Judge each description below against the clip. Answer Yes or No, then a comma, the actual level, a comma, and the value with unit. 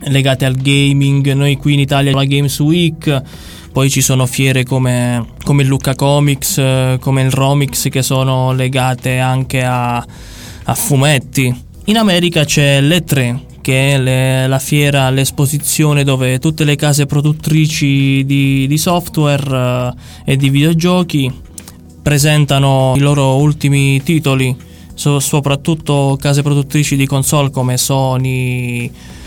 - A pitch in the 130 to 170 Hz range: Yes, low, 135 Hz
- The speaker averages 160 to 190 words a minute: No, average, 130 wpm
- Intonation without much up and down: Yes, narrow, 1.8 semitones